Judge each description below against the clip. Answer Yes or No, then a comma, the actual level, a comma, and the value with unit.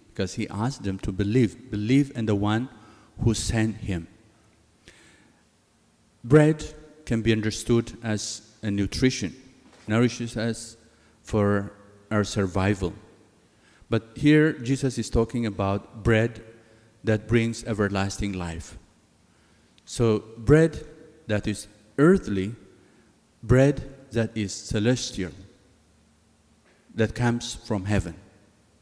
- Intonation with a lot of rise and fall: No, average, 2.8 semitones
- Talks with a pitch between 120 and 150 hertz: No, low, 110 Hz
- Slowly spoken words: Yes, slow, 100 wpm